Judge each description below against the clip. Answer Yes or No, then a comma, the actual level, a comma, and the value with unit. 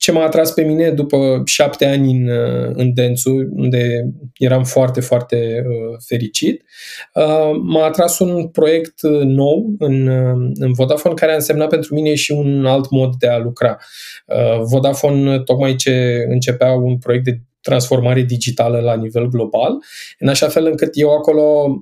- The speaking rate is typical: Yes, average, 150 wpm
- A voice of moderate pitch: No, low, 130 Hz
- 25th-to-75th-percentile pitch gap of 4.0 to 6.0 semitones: No, average, 3.4 semitones